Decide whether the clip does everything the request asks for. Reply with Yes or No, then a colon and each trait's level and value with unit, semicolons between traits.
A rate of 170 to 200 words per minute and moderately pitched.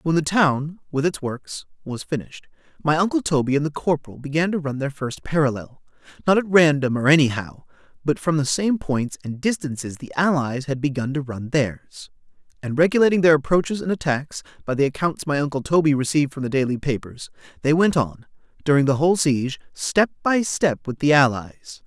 Yes: average, 185 wpm; medium, 145 Hz